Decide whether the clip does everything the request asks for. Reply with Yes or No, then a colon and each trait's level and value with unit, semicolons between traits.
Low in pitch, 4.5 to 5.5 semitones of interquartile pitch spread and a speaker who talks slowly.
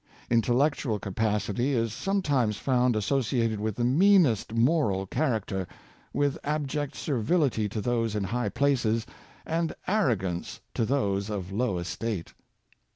Yes: low, 115 Hz; average, 4.9 semitones; slow, 130 wpm